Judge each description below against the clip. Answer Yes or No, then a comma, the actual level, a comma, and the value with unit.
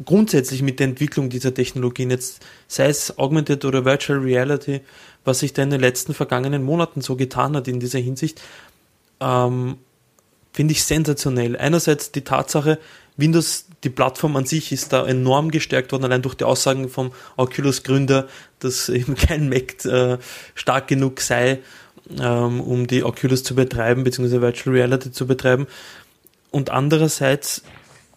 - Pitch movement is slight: Yes, narrow, 2.1 semitones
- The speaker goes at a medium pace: Yes, average, 150 wpm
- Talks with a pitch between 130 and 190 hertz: Yes, low, 135 Hz